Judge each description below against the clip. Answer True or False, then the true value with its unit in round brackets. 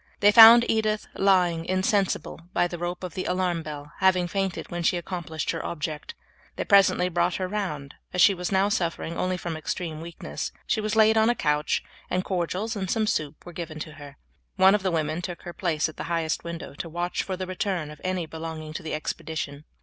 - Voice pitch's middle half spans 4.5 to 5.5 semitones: False (3.0 semitones)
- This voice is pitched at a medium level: True (175 Hz)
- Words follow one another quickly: True (215 wpm)